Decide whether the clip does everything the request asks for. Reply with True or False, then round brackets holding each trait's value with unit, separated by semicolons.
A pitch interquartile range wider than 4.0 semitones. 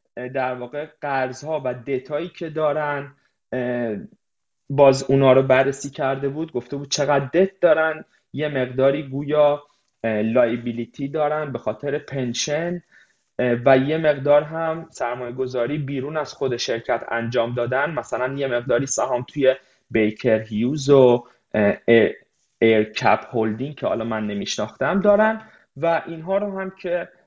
False (3.5 semitones)